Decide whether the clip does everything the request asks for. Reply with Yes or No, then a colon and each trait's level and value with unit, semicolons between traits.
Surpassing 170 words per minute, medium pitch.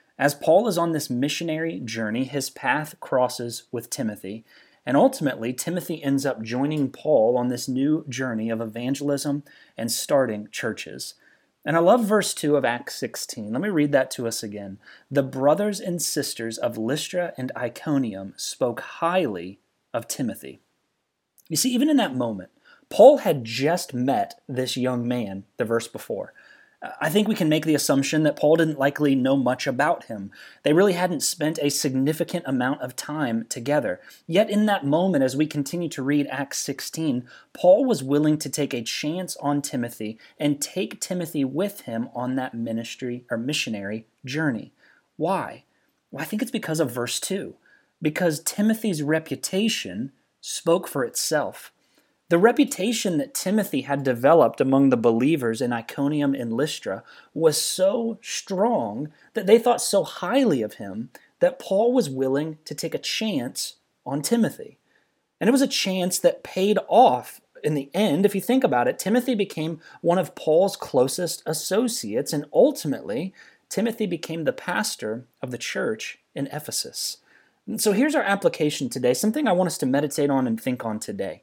No: average, 165 wpm; medium, 150 Hz